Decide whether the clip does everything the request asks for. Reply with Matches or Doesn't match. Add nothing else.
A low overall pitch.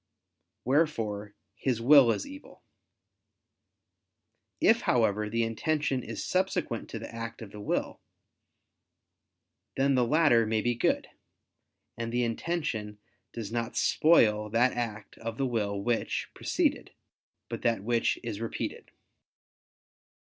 Matches